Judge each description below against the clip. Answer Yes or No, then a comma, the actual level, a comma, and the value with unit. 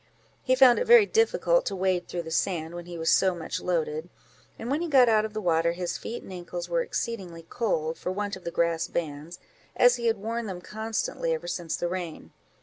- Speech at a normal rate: No, fast, 225 wpm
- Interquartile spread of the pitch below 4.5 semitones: No, wide, 5.5 semitones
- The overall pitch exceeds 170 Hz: Yes, medium, 185 Hz